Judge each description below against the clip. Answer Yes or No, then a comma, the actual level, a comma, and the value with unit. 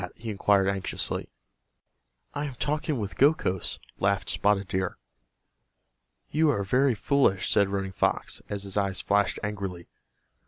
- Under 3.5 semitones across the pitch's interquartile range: No, average, 5.2 semitones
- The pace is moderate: No, slow, 130 wpm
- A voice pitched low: Yes, low, 100 Hz